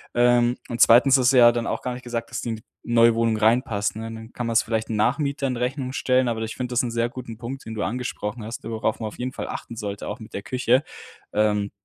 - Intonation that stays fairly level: Yes, narrow, 2.0 semitones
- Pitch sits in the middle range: No, low, 115 Hz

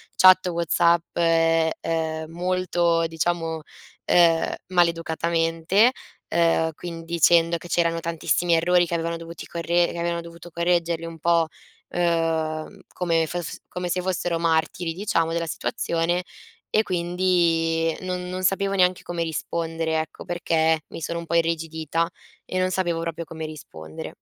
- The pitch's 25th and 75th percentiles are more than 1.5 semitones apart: No, narrow, 1.1 semitones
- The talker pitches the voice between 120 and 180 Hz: Yes, medium, 170 Hz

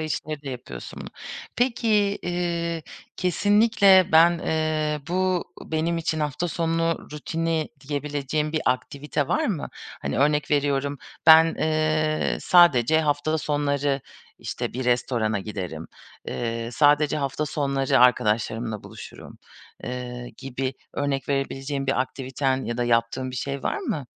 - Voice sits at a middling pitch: Yes, medium, 145 Hz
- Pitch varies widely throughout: No, average, 3.5 semitones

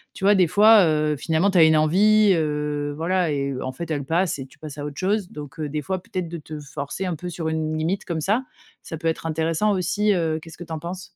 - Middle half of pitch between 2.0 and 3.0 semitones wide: No, average, 3.5 semitones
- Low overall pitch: No, medium, 160 Hz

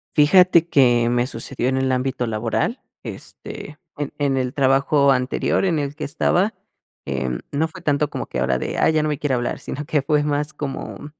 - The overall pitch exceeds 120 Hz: Yes, medium, 140 Hz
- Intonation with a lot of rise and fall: No, average, 2.8 semitones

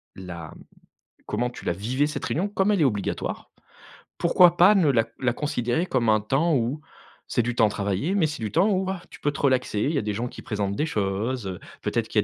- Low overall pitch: Yes, low, 125 Hz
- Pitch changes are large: Yes, wide, 7.3 semitones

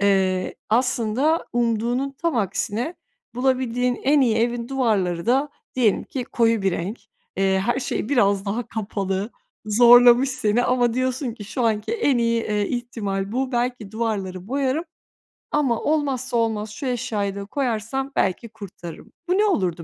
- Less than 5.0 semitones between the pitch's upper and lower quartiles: Yes, average, 3.9 semitones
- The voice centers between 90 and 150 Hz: No, high, 235 Hz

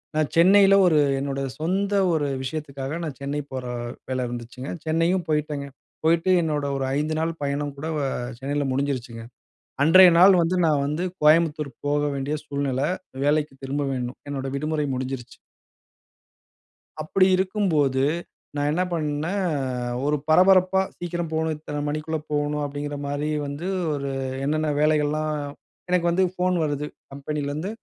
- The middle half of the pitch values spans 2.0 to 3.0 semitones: Yes, average, 2.7 semitones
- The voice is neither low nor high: Yes, medium, 150 Hz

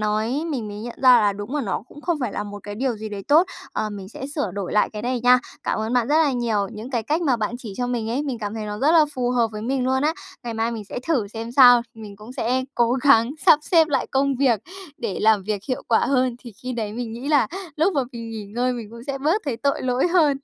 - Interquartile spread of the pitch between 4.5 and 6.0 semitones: No, average, 3.8 semitones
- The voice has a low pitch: No, high, 240 Hz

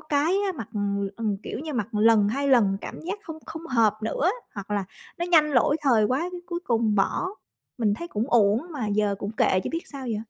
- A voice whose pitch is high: Yes, high, 230 Hz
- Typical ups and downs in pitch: No, wide, 6.4 semitones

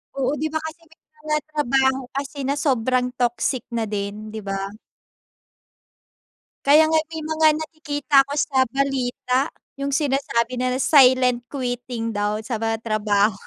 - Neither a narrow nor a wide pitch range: Yes, average, 3.8 semitones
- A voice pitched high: Yes, very high, 260 Hz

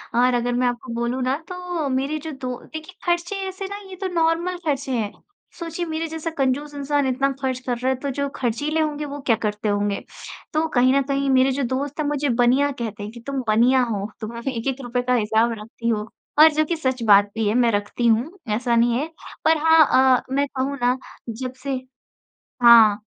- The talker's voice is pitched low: No, very high, 260 Hz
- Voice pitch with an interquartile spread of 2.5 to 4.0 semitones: Yes, average, 3.7 semitones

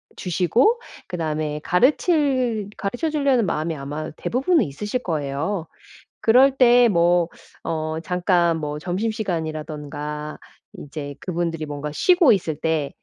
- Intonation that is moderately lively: No, wide, 7.3 semitones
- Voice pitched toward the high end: No, medium, 175 Hz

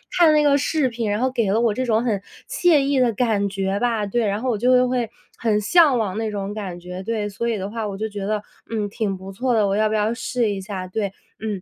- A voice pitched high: Yes, high, 220 Hz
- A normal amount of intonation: Yes, average, 3.4 semitones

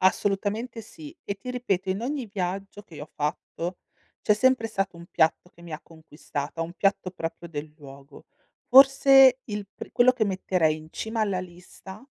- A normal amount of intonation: Yes, average, 5.0 semitones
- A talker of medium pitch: No, high, 195 Hz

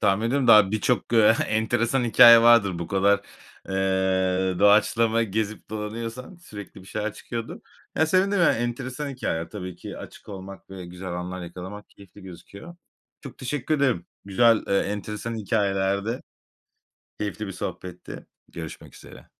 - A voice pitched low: Yes, low, 105 Hz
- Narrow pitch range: No, average, 3.6 semitones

